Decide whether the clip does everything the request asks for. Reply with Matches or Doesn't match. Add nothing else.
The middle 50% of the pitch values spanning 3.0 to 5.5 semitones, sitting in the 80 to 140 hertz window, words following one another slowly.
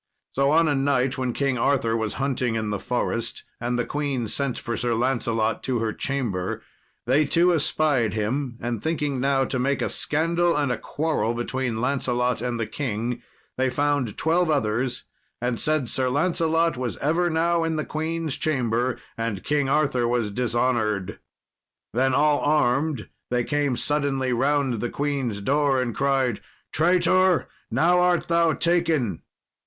Doesn't match